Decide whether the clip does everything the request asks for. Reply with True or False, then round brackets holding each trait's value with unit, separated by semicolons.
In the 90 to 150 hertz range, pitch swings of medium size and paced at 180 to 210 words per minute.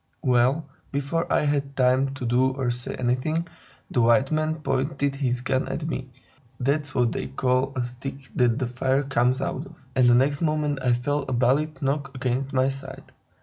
False (135 Hz; 2.0 semitones; 190 wpm)